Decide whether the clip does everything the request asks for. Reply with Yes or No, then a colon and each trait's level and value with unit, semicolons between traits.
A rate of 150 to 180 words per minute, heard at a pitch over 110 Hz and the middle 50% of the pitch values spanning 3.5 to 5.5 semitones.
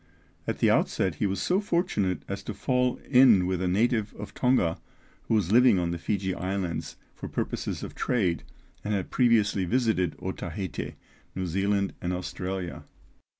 No: average, 160 wpm; low, 100 Hz; average, 4.0 semitones